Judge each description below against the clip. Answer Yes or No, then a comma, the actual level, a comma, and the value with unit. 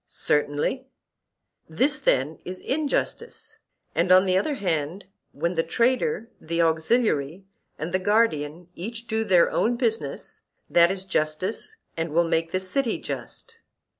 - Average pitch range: No, wide, 6.1 semitones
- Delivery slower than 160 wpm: Yes, slow, 135 wpm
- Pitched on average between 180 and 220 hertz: Yes, medium, 185 Hz